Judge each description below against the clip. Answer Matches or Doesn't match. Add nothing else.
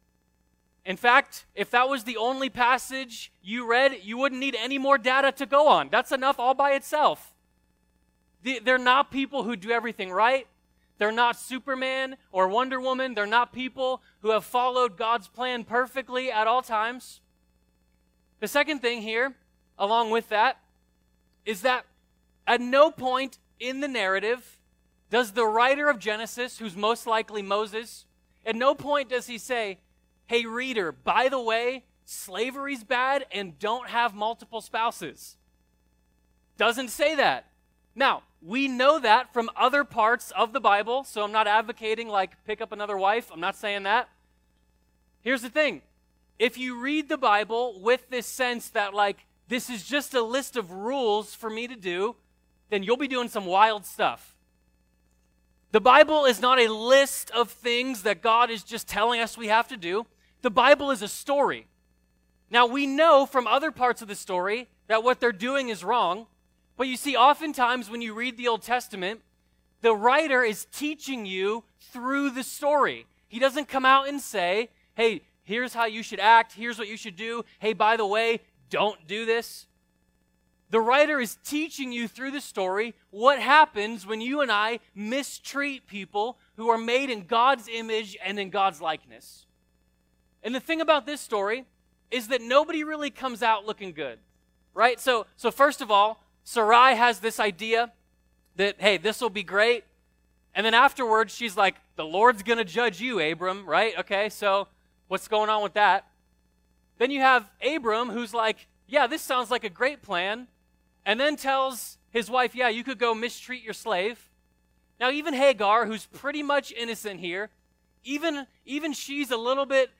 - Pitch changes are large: Doesn't match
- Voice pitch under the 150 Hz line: Doesn't match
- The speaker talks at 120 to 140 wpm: Doesn't match